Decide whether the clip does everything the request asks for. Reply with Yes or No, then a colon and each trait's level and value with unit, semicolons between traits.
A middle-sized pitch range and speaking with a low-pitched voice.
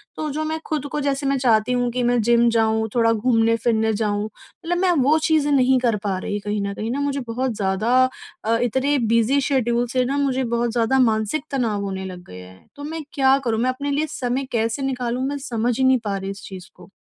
No: average, 3.7 semitones; high, 240 Hz